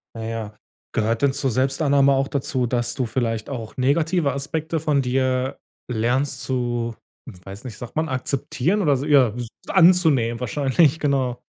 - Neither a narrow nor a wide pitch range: Yes, average, 3.0 semitones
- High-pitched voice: No, low, 130 Hz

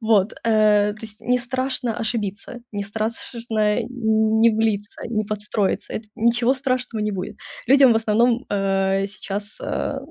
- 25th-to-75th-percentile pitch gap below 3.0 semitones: Yes, narrow, 2.4 semitones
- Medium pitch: No, high, 220 Hz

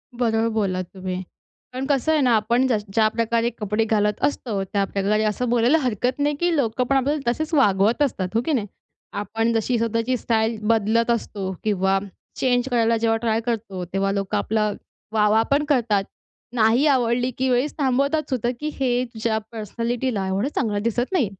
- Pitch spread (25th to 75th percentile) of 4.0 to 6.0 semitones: No, average, 3.1 semitones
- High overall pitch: Yes, high, 230 Hz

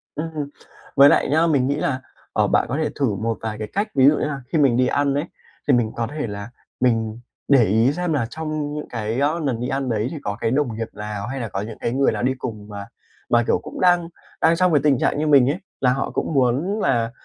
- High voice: No, low, 135 Hz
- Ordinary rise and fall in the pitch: Yes, average, 4.7 semitones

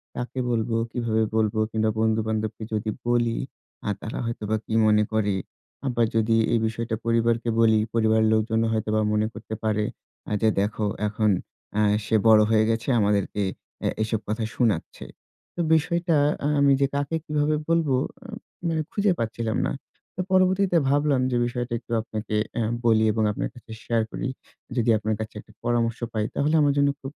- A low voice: Yes, low, 115 Hz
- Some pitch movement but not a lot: No, narrow, 2.2 semitones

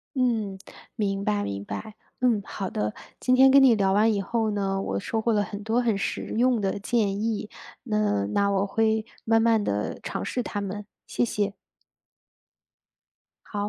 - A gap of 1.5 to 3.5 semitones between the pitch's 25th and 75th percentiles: Yes, narrow, 2.4 semitones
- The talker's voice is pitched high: Yes, high, 210 Hz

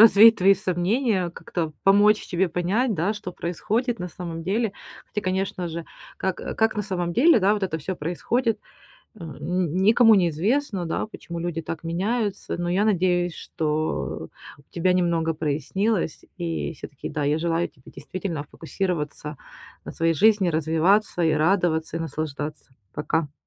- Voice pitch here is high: No, medium, 175 Hz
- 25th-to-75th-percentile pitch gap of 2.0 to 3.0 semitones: No, average, 3.8 semitones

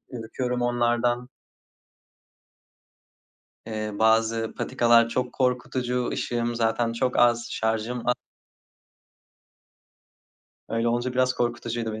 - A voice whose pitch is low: Yes, low, 120 Hz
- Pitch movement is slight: Yes, narrow, 1.4 semitones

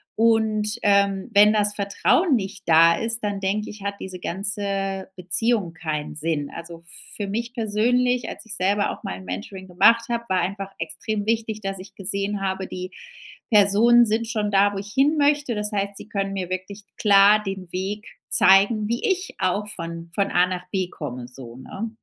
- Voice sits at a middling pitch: No, high, 200 Hz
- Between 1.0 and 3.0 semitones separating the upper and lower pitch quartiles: Yes, narrow, 2.6 semitones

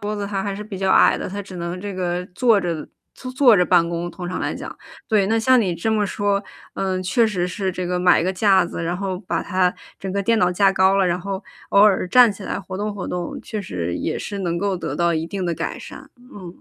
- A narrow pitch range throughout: Yes, narrow, 2.3 semitones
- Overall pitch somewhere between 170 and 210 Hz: Yes, high, 190 Hz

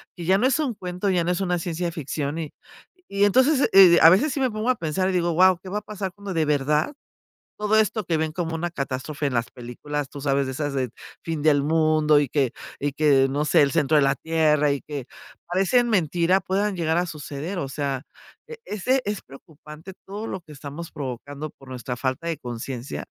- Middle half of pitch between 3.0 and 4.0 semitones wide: No, average, 4.8 semitones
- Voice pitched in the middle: Yes, medium, 160 Hz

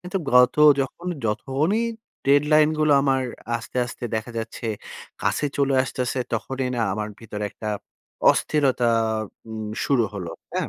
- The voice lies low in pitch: Yes, low, 130 Hz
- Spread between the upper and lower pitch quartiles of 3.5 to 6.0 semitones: Yes, average, 4.1 semitones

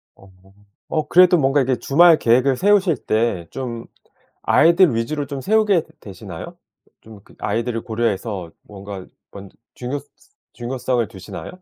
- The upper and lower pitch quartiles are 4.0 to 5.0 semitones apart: No, wide, 5.5 semitones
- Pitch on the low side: Yes, low, 125 Hz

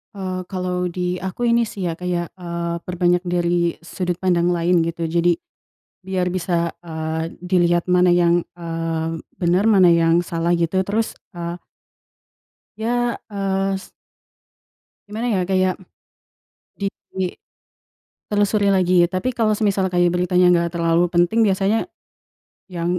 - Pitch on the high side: No, medium, 180 Hz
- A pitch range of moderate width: No, narrow, 2.0 semitones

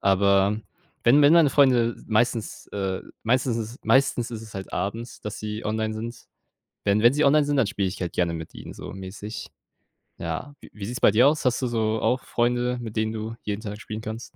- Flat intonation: No, average, 3.1 semitones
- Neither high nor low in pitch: No, low, 110 Hz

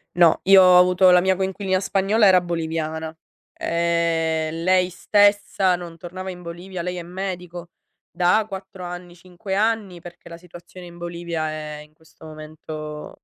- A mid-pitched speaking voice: Yes, medium, 175 Hz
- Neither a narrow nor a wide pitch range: No, narrow, 2.0 semitones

